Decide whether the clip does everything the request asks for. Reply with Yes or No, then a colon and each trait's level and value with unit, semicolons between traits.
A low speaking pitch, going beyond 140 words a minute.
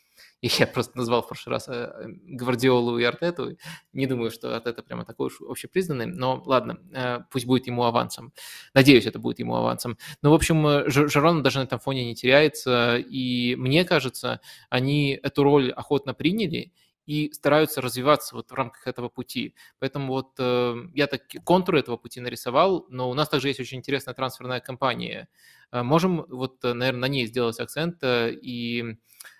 Yes: low, 130 Hz; fast, 160 wpm